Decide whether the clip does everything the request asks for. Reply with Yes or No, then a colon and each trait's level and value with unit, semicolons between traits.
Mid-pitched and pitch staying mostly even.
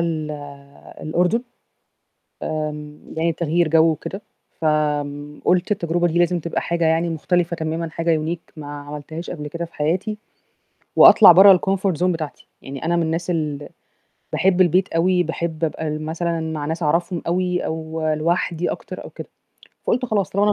Yes: medium, 165 Hz; narrow, 2.3 semitones